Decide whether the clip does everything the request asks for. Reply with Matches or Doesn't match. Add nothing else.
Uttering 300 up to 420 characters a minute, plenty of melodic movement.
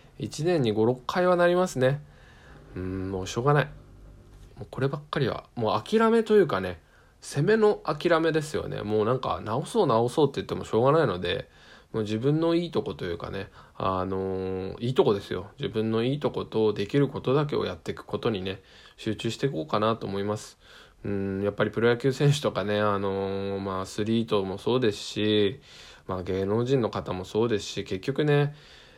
Matches